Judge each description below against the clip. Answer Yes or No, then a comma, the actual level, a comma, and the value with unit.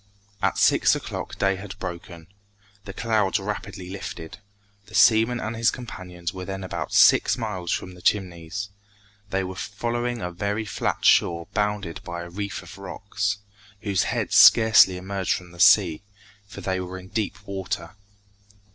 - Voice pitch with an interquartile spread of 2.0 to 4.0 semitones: Yes, narrow, 2.5 semitones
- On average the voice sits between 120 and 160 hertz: No, very low, 95 Hz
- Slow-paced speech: No, average, 155 wpm